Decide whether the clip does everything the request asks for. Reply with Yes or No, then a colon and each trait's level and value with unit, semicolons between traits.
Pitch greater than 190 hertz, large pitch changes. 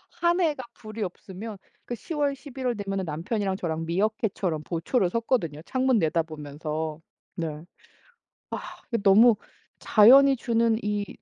Yes: high, 205 Hz; wide, 6.5 semitones